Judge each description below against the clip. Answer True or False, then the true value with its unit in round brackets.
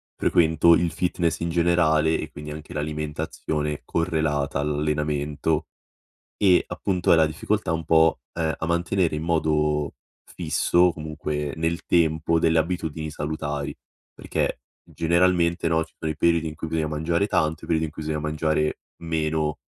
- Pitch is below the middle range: True (80 Hz)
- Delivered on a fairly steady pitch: True (1.6 semitones)